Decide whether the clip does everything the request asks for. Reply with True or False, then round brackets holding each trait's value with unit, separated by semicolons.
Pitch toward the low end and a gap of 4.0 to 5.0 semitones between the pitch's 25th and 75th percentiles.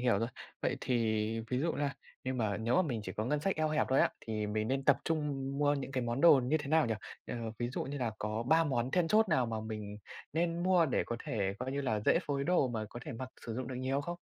True (130 Hz; 4.6 semitones)